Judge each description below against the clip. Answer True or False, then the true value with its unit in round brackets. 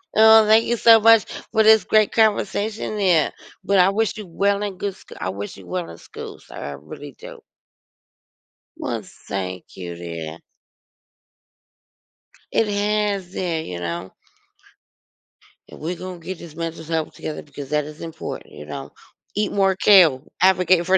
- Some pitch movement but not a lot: False (6.2 semitones)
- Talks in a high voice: False (180 Hz)